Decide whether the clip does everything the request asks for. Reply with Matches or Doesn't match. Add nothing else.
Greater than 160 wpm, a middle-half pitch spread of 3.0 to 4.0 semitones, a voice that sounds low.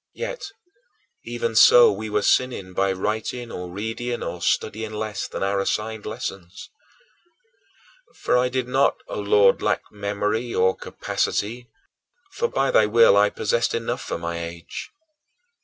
Doesn't match